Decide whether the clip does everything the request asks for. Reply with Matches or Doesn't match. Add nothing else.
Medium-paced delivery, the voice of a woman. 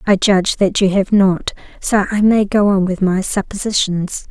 Matches